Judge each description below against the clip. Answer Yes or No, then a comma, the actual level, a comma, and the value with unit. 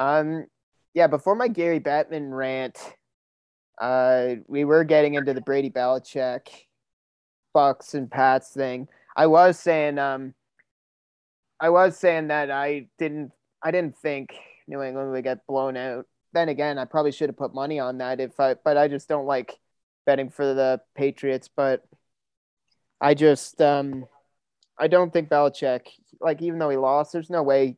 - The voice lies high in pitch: No, medium, 140 Hz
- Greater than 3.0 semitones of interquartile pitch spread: No, average, 2.7 semitones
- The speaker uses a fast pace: No, average, 160 wpm